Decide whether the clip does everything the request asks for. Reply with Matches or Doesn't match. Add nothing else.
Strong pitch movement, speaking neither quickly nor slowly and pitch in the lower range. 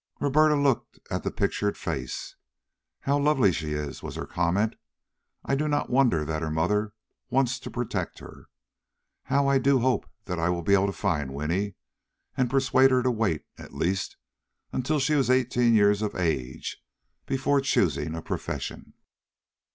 Matches